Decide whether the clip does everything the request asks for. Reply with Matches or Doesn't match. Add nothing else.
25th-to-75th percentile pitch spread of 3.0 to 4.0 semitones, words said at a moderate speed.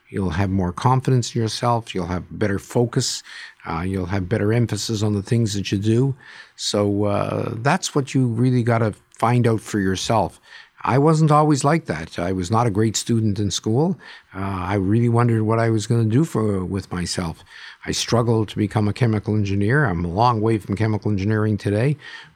Matches